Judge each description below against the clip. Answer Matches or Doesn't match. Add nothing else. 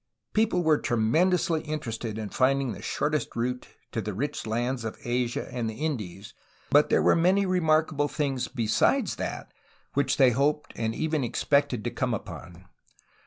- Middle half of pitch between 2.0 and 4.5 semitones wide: Doesn't match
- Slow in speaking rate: Doesn't match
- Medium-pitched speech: Doesn't match